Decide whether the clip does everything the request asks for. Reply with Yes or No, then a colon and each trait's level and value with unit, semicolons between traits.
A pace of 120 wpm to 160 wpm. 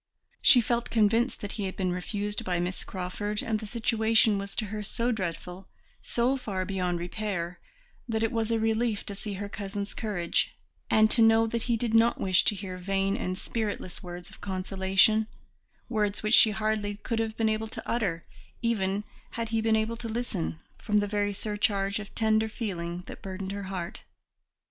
No: average, 185 wpm